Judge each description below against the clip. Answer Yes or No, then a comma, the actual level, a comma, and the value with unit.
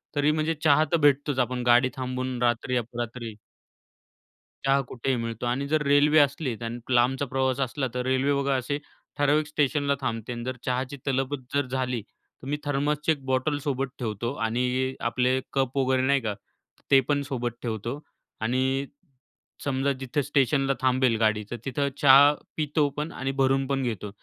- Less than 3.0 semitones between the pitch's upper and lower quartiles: Yes, narrow, 2.4 semitones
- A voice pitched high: No, low, 130 Hz